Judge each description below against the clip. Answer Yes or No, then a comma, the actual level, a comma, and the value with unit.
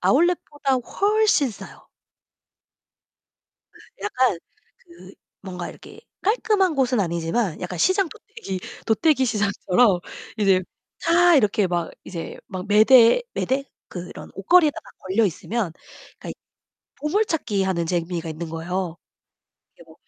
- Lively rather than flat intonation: Yes, wide, 8.8 semitones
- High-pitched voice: Yes, high, 210 Hz